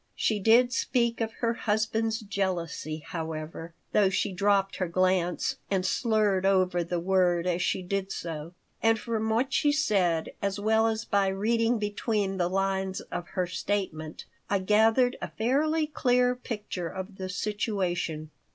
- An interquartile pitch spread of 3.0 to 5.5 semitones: Yes, average, 3.6 semitones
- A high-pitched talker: Yes, high, 200 Hz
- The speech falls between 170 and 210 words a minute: No, average, 150 wpm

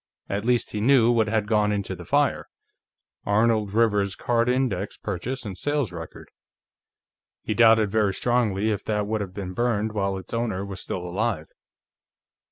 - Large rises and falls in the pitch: No, average, 3.0 semitones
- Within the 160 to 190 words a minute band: Yes, average, 165 wpm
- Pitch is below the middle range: Yes, low, 105 Hz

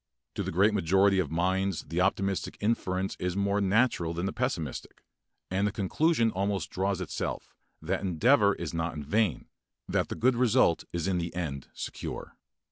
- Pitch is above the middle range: No, very low, 95 Hz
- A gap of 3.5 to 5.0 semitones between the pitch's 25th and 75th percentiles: No, average, 2.9 semitones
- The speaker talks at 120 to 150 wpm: No, average, 170 wpm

